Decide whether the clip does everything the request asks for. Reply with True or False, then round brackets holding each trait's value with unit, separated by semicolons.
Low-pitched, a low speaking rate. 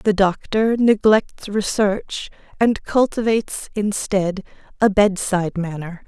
False (205 Hz; 100 wpm)